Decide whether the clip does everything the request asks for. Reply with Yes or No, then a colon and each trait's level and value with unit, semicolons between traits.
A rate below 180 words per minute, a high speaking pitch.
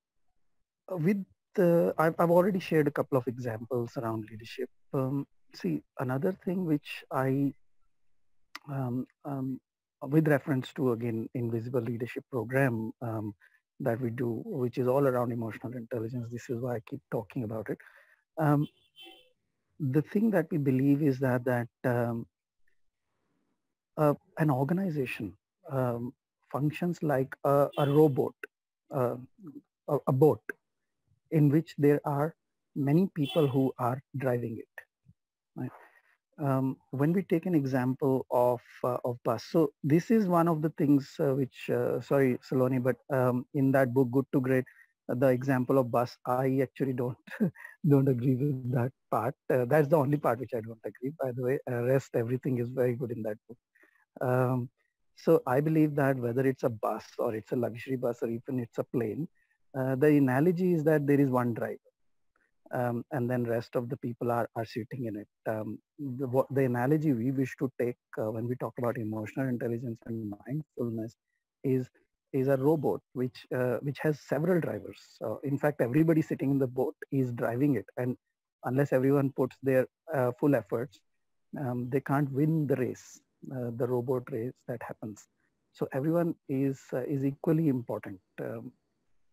No: average, 165 wpm; low, 135 Hz